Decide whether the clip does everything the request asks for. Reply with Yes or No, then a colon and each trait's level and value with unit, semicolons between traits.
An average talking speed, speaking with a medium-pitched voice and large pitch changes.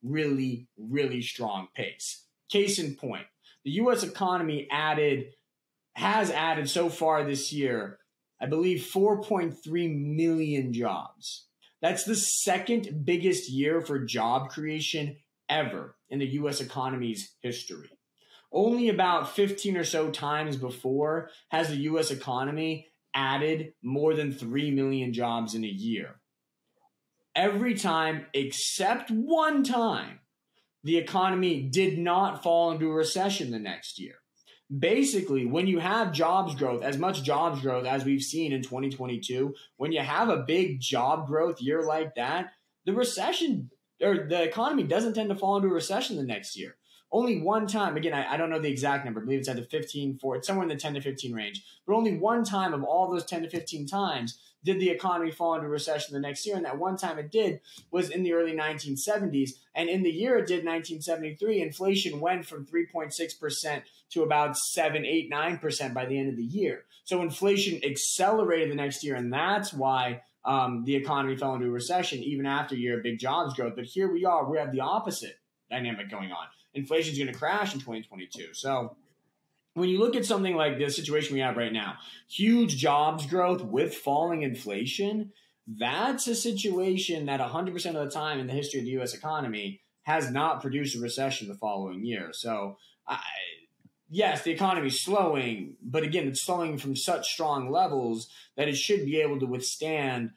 No: average, 175 wpm; medium, 155 Hz; average, 4.9 semitones